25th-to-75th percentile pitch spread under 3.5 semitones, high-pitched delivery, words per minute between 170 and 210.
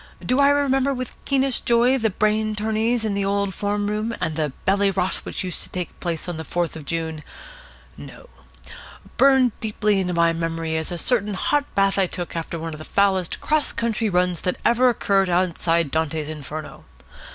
No: average, 5.3 semitones; high, 195 Hz; average, 195 wpm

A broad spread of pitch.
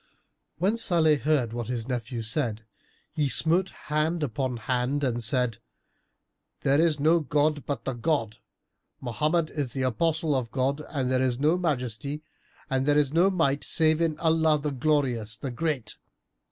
No: average, 3.9 semitones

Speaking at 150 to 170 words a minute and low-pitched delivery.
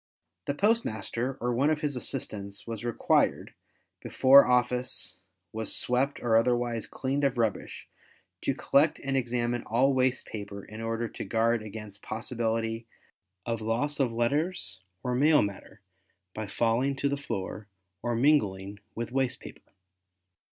No: average, 140 wpm; low, 120 Hz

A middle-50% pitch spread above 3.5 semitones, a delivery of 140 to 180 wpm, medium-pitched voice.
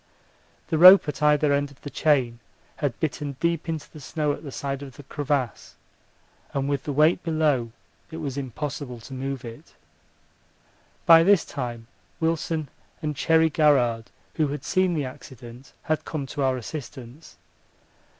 No: average, 3.0 semitones; average, 160 wpm; medium, 145 Hz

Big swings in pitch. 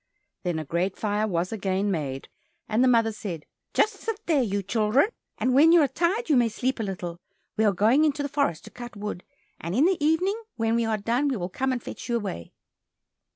Yes: wide, 6.3 semitones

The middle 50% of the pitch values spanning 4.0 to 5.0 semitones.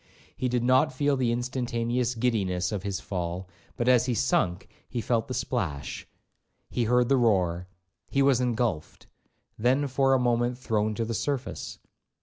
No: average, 3.4 semitones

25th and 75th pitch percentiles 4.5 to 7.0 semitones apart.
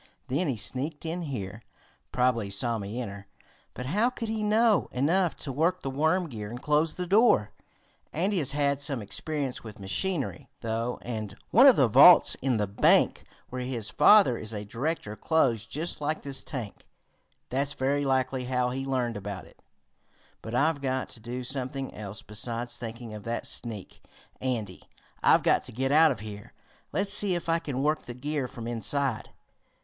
Yes: average, 5.1 semitones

